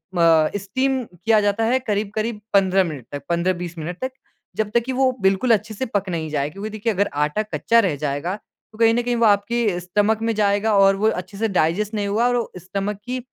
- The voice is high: Yes, high, 205 Hz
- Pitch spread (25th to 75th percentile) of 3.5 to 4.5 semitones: Yes, average, 4.0 semitones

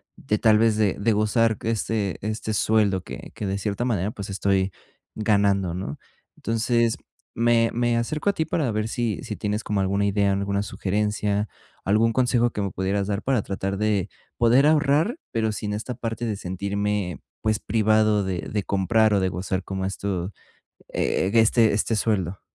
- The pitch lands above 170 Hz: No, low, 105 Hz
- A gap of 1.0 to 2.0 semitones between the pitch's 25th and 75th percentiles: No, narrow, 2.5 semitones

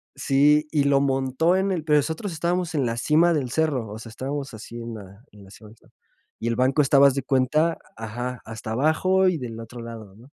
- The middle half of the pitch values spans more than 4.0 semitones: Yes, average, 5.0 semitones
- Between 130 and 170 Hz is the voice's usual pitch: Yes, low, 135 Hz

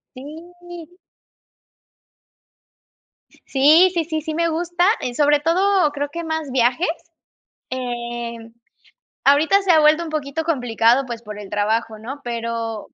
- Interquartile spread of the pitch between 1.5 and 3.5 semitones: No, wide, 5.6 semitones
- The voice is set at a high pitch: Yes, very high, 290 Hz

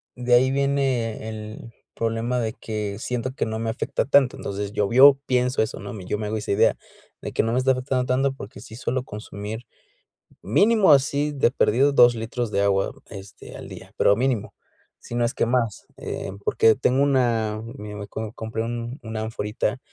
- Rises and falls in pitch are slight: No, average, 3.0 semitones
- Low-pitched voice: Yes, low, 115 Hz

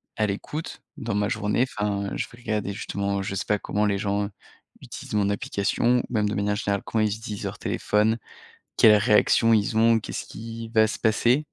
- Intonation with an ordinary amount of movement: No, narrow, 1.8 semitones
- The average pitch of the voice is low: Yes, low, 105 Hz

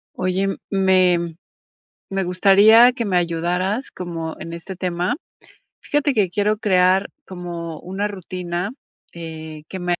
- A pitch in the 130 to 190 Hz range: Yes, medium, 185 Hz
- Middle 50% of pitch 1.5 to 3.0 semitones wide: Yes, narrow, 2.4 semitones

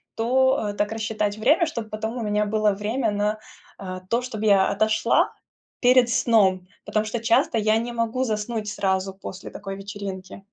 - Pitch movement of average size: No, narrow, 2.3 semitones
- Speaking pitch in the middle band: No, high, 215 Hz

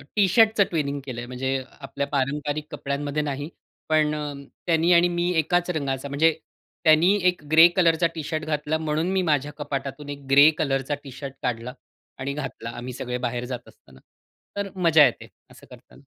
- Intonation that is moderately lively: Yes, average, 3.0 semitones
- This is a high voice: No, medium, 150 Hz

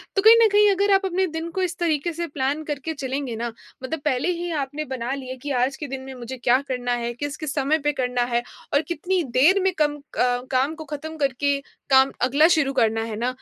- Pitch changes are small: No, average, 3.9 semitones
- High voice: Yes, very high, 285 Hz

